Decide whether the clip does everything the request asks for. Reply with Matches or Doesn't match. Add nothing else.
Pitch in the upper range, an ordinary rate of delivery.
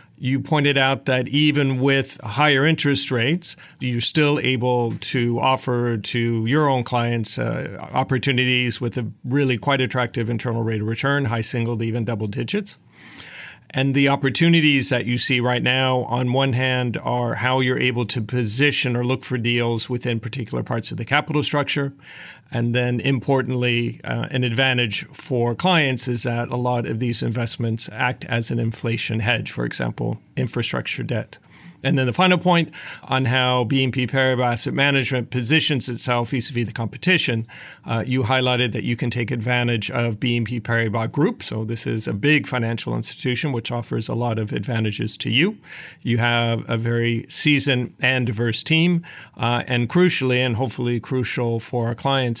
Doesn't match